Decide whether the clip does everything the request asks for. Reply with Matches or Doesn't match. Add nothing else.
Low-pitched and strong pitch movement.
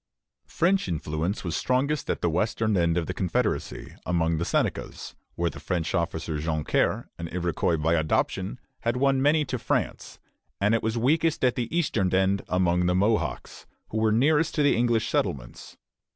Matches